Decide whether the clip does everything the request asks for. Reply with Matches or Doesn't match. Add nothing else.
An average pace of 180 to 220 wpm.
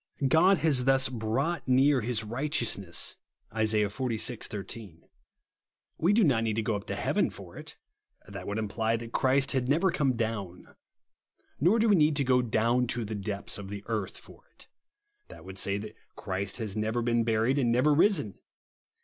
Matches